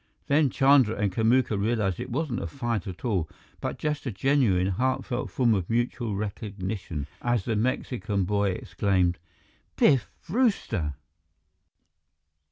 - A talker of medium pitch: No, low, 110 Hz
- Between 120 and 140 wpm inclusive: Yes, slow, 135 wpm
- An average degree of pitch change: Yes, average, 4.9 semitones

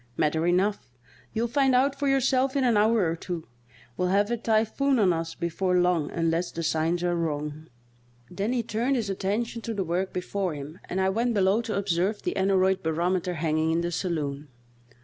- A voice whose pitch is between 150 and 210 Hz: Yes, high, 190 Hz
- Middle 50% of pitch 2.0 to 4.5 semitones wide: No, average, 5.1 semitones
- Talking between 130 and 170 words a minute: No, average, 190 wpm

